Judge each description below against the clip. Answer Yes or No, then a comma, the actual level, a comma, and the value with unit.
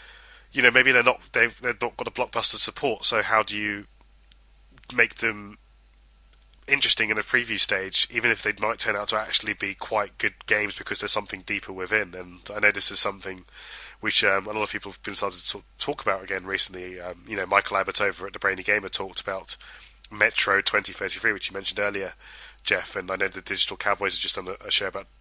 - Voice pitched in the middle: No, very low, 95 Hz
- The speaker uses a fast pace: Yes, fast, 215 wpm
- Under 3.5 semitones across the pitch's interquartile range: Yes, narrow, 2.5 semitones